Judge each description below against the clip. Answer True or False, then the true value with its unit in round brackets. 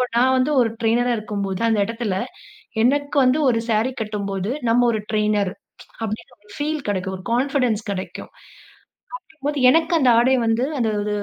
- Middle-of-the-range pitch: False (230 Hz)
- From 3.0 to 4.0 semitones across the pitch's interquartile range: True (3.7 semitones)